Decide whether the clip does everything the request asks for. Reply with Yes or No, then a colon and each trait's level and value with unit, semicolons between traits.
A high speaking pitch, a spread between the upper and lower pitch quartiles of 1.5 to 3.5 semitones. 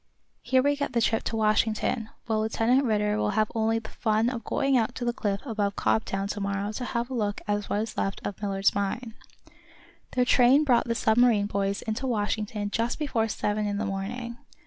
Yes: high, 220 Hz; narrow, 2.5 semitones